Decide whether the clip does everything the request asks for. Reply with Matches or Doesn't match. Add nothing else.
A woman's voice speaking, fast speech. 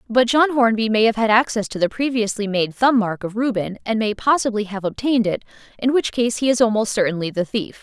Matches